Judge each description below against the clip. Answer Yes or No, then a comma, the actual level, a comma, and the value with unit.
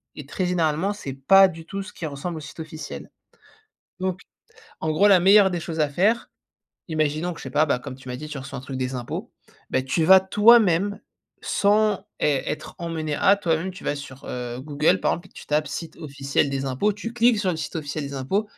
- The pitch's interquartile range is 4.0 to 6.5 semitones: Yes, average, 5.1 semitones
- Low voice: No, medium, 160 Hz